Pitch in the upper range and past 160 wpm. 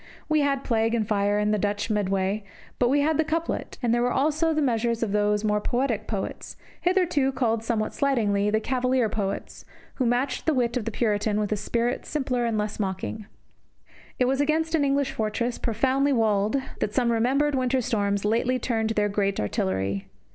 Yes: high, 230 Hz; average, 190 wpm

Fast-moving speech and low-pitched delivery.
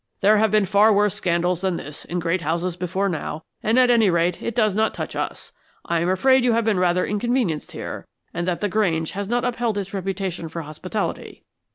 No: fast, 215 wpm; high, 190 Hz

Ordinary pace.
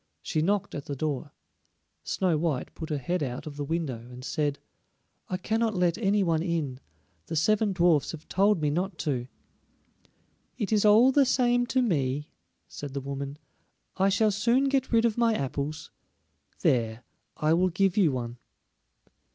Yes: average, 165 wpm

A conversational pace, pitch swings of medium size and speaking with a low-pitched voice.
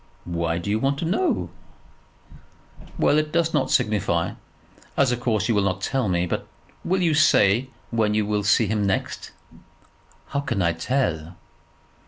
No: average, 165 wpm; wide, 6.5 semitones; low, 110 Hz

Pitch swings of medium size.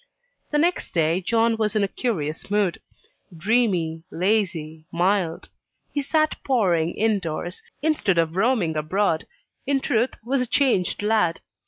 No: wide, 5.8 semitones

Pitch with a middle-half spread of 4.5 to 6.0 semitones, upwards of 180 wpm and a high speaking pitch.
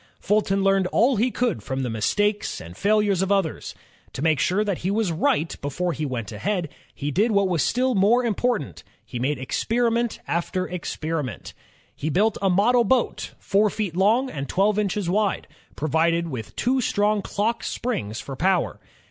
No: average, 5.1 semitones; average, 175 wpm; high, 195 Hz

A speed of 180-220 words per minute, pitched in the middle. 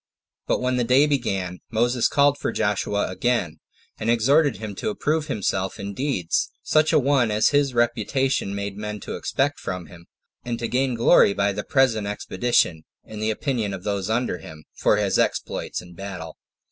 No: average, 185 wpm; low, 110 Hz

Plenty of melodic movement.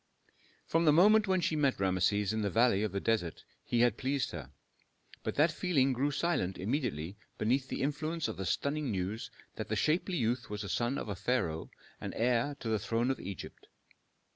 Yes: wide, 6.1 semitones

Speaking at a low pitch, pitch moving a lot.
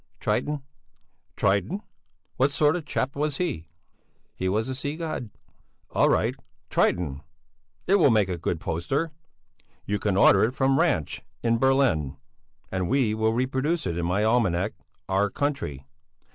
Yes: low, 115 Hz; wide, 7.1 semitones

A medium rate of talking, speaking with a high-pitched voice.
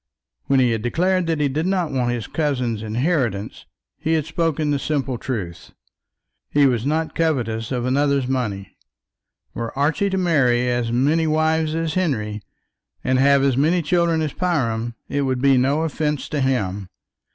No: average, 165 wpm; medium, 140 Hz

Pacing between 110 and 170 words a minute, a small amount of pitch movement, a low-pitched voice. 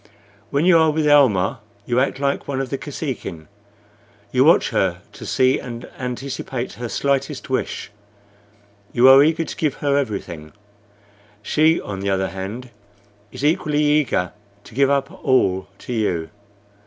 No: average, 155 wpm; average, 4.9 semitones; low, 130 Hz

